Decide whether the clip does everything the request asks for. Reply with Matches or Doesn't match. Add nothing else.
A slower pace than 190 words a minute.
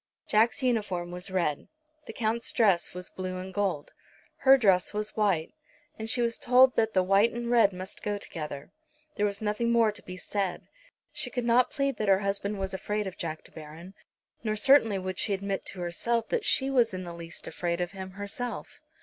Doesn't match